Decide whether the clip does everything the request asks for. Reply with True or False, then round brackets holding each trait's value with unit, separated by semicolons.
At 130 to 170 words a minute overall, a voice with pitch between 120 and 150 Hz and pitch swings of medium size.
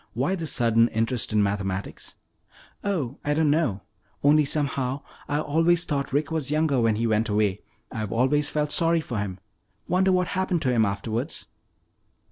False (165 wpm; 140 Hz; 5.7 semitones)